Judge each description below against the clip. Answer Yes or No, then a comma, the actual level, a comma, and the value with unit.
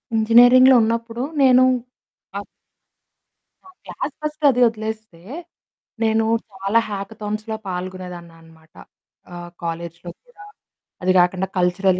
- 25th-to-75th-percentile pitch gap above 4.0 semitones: Yes, average, 4.5 semitones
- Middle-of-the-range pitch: No, high, 210 Hz